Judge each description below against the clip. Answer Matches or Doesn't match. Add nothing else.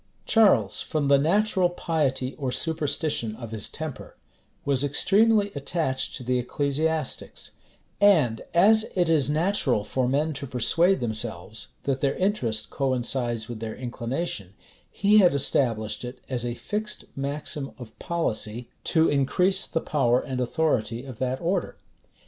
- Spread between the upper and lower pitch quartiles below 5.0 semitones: Doesn't match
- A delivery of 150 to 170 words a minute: Doesn't match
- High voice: Doesn't match